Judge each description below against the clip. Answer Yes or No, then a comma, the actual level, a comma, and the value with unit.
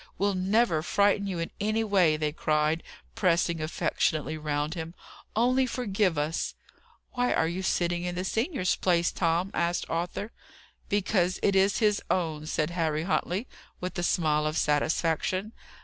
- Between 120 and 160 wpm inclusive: Yes, average, 150 wpm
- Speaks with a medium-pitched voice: Yes, medium, 175 Hz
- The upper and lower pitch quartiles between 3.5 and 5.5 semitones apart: Yes, average, 3.8 semitones